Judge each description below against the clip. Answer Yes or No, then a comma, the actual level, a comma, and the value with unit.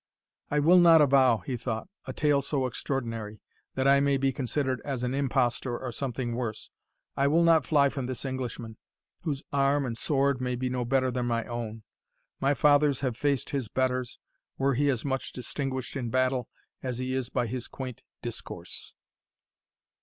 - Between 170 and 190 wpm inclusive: Yes, average, 175 wpm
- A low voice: Yes, low, 130 Hz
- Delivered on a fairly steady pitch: Yes, narrow, 2.2 semitones